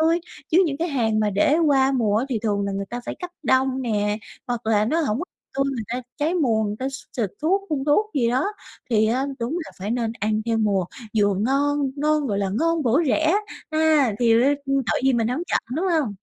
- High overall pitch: Yes, very high, 255 Hz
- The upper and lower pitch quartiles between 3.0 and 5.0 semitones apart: No, wide, 5.5 semitones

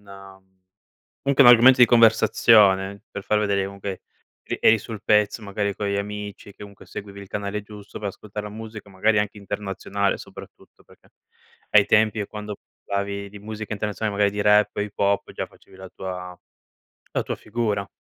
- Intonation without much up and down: Yes, narrow, 1.1 semitones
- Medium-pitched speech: No, low, 100 Hz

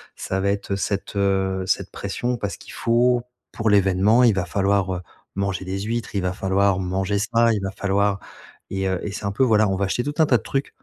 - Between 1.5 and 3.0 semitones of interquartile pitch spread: Yes, narrow, 2.6 semitones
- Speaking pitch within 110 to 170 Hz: No, low, 100 Hz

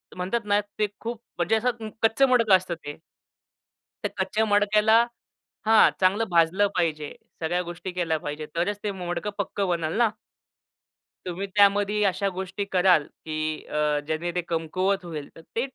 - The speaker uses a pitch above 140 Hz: Yes, medium, 185 Hz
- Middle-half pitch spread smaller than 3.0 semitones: No, average, 3.6 semitones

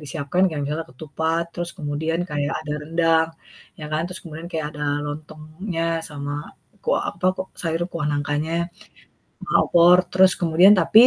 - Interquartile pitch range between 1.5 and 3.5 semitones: Yes, narrow, 2.5 semitones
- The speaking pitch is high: No, medium, 160 Hz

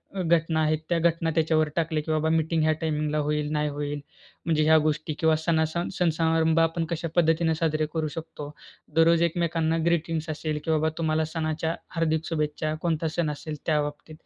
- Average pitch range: No, narrow, 1.1 semitones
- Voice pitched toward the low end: No, medium, 160 Hz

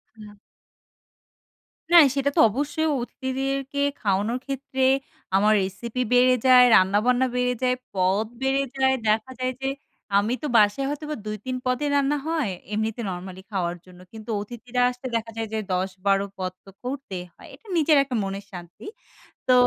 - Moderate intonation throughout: Yes, average, 4.9 semitones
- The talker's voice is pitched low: No, high, 240 Hz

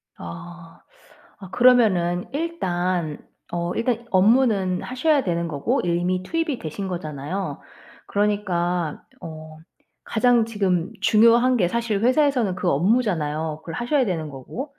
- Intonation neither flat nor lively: No, wide, 5.7 semitones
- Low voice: No, medium, 185 Hz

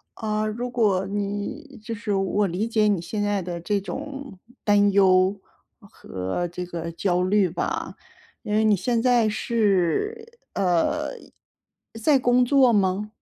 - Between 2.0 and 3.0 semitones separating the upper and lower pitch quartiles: No, average, 3.9 semitones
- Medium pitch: No, high, 205 Hz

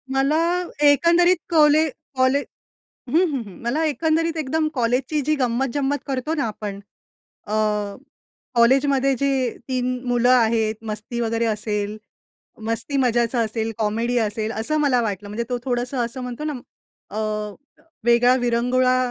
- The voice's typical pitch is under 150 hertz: No, very high, 250 Hz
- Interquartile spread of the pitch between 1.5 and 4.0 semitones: Yes, average, 3.5 semitones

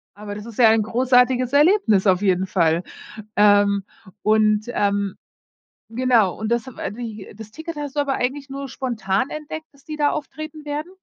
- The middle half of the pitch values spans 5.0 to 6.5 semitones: Yes, wide, 5.6 semitones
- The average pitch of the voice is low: No, high, 235 Hz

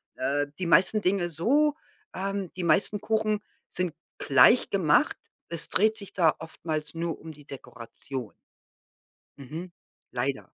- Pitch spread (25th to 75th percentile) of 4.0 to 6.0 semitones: Yes, average, 5.1 semitones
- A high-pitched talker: No, medium, 170 Hz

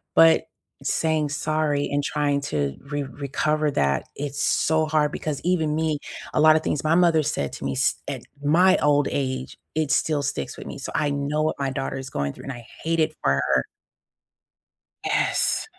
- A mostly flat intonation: Yes, narrow, 2.1 semitones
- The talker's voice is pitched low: No, medium, 150 Hz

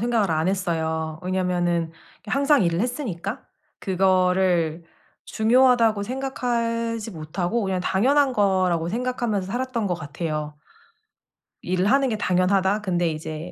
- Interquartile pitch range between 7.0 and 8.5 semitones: No, average, 5.1 semitones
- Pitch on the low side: No, high, 190 Hz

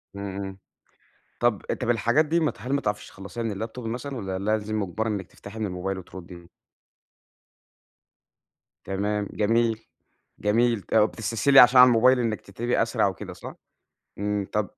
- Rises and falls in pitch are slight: No, average, 3.2 semitones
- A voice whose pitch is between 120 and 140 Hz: No, low, 110 Hz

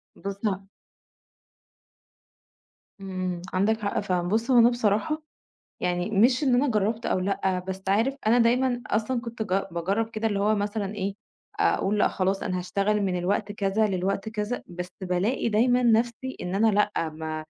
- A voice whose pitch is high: Yes, high, 205 Hz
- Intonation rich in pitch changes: No, average, 3.2 semitones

